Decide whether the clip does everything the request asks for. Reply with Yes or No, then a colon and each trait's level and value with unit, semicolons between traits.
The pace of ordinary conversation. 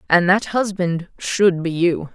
Yes: average, 170 wpm